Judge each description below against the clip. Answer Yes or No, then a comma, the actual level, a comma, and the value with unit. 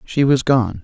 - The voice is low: Yes, low, 130 Hz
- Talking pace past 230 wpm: No, fast, 215 wpm